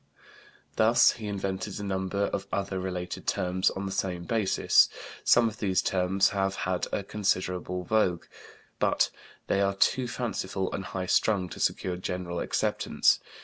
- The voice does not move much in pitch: Yes, narrow, 1.7 semitones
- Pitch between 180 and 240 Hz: No, very low, 95 Hz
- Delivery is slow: No, average, 150 wpm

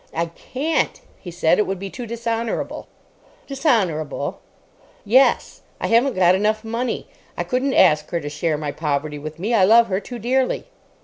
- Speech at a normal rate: Yes, average, 170 wpm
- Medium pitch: No, high, 210 Hz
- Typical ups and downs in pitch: No, wide, 6.2 semitones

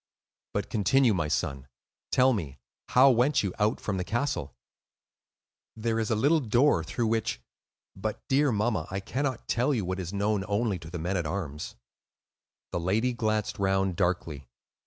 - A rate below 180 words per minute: Yes, average, 160 wpm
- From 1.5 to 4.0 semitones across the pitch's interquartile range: No, average, 5.1 semitones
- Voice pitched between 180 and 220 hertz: No, low, 105 Hz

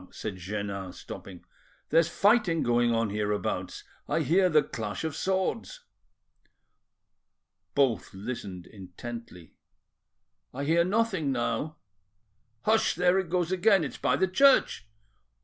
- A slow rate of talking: Yes, slow, 115 wpm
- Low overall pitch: No, medium, 145 Hz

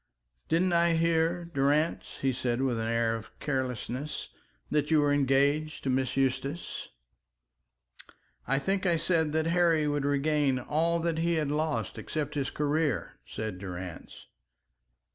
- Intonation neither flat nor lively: Yes, average, 3.5 semitones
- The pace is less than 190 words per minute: Yes, average, 145 wpm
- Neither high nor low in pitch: Yes, medium, 145 Hz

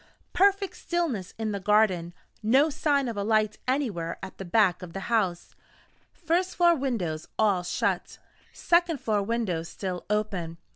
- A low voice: No, high, 215 Hz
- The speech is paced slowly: No, average, 150 wpm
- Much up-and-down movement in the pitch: Yes, wide, 7.2 semitones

